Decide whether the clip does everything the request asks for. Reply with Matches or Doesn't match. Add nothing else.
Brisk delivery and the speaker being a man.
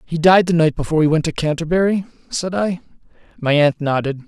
Doesn't match